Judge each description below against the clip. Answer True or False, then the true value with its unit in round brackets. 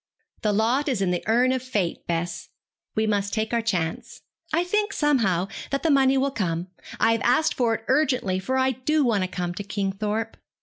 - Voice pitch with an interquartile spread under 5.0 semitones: False (5.3 semitones)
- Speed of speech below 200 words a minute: False (205 wpm)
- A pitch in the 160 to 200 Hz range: False (225 Hz)